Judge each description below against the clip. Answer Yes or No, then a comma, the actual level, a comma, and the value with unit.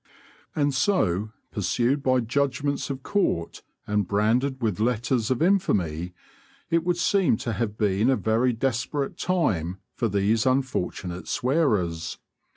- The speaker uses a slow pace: Yes, slow, 130 wpm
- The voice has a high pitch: No, low, 120 Hz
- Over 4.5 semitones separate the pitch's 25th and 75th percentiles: Yes, average, 5.3 semitones